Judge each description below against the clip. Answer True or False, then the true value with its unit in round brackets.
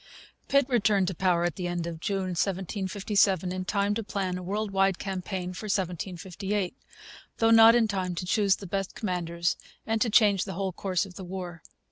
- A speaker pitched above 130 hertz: True (190 Hz)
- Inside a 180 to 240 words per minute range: True (190 wpm)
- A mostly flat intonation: True (2.2 semitones)